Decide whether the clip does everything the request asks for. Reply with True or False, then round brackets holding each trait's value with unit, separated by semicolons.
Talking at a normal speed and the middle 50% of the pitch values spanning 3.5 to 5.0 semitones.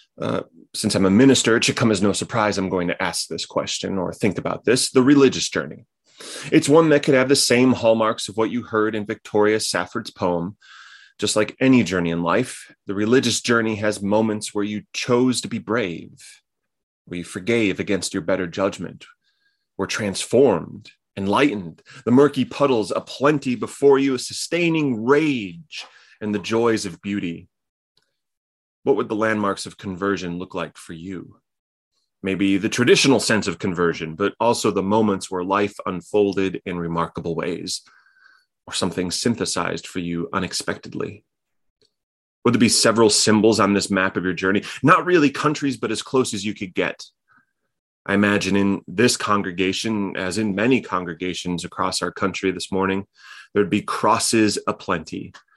True (165 wpm; 3.8 semitones)